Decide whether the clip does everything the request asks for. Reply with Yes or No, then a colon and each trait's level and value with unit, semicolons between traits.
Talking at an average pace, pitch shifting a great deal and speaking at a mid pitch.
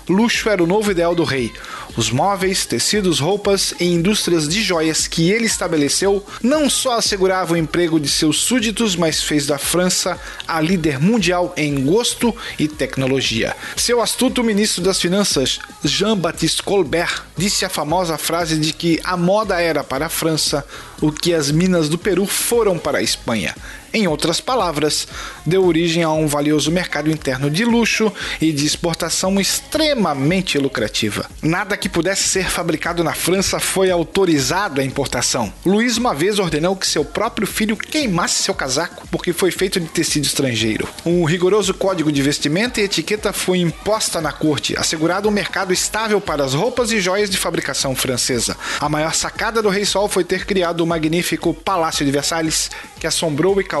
No: average, 170 wpm; average, 4.2 semitones; medium, 175 Hz